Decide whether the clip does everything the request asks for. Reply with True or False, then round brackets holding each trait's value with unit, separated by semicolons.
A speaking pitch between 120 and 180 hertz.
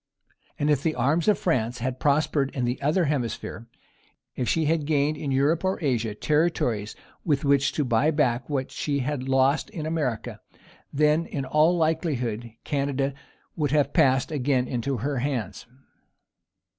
True (140 Hz)